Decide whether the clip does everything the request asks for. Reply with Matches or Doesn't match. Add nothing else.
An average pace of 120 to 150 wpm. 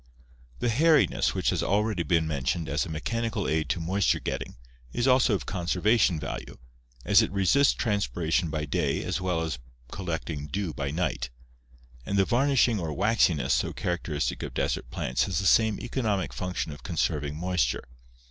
Doesn't match